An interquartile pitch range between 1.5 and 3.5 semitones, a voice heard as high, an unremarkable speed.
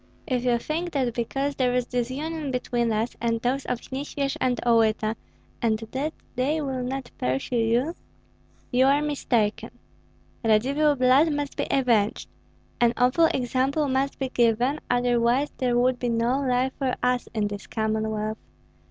Yes: average, 2.8 semitones; very high, 250 Hz; average, 150 wpm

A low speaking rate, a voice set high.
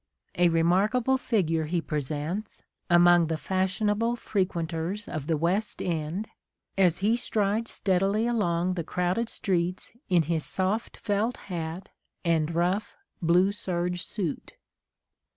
No: slow, 120 wpm; medium, 180 Hz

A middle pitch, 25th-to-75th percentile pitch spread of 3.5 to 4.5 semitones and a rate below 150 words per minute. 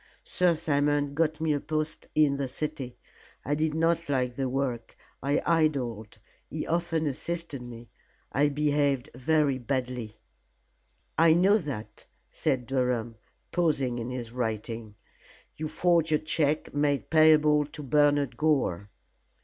Yes: medium, 145 Hz; average, 3.8 semitones; slow, 135 wpm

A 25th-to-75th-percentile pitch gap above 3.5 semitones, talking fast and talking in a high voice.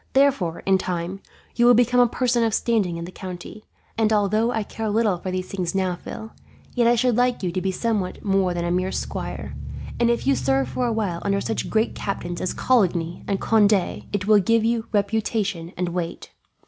Yes: average, 3.9 semitones; fast, 210 wpm; high, 200 Hz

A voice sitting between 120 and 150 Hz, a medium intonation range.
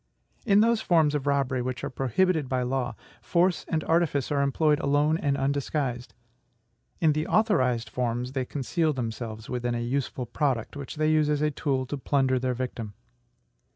Yes: medium, 140 Hz; average, 3.5 semitones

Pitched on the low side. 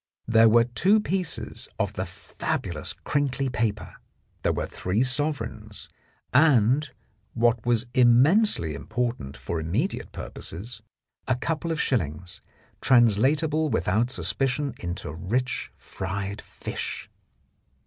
Yes: low, 120 Hz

